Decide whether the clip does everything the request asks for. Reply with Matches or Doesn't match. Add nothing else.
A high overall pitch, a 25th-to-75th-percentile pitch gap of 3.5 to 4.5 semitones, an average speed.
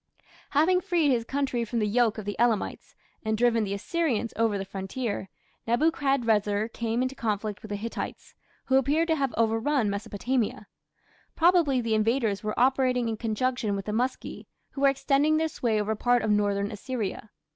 Matches